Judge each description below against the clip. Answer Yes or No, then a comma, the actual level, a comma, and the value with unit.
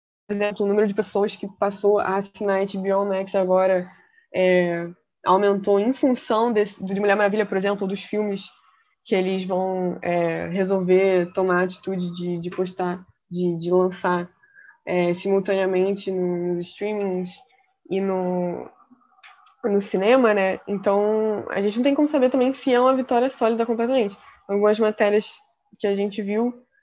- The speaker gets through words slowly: No, average, 150 wpm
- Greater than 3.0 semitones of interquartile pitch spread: No, average, 2.7 semitones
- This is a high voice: Yes, high, 200 Hz